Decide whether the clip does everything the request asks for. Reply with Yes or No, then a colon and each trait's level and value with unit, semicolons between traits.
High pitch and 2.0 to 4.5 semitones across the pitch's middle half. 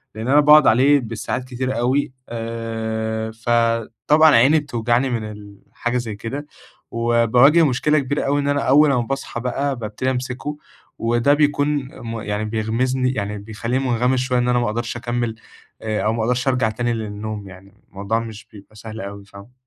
No: low, 120 Hz; average, 2.9 semitones